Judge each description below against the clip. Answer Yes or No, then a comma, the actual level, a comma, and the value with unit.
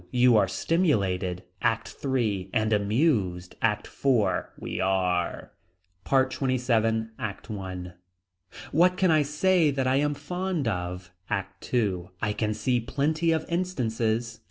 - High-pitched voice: No, low, 115 Hz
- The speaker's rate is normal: No, slow, 130 wpm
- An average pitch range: No, wide, 6.4 semitones